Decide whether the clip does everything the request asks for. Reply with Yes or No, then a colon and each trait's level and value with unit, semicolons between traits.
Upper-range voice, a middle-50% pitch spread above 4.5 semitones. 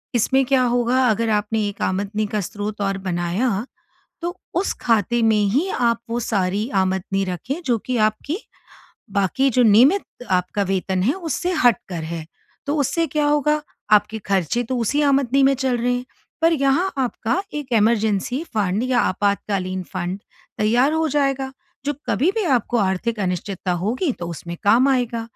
Yes: high, 230 Hz; average, 5.1 semitones